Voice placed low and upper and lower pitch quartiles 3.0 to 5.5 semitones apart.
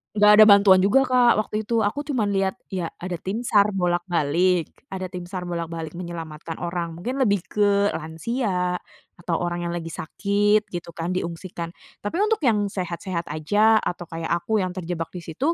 No: medium, 185 Hz; average, 3.3 semitones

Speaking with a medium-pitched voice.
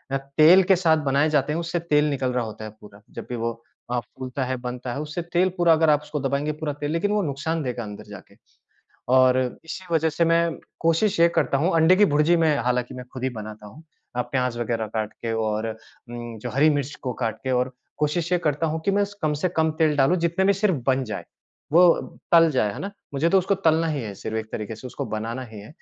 Yes: medium, 145 Hz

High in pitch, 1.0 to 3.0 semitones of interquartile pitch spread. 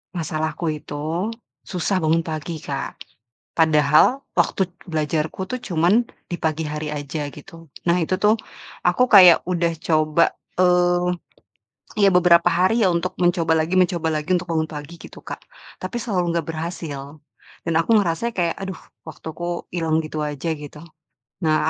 No: medium, 165 Hz; narrow, 2.4 semitones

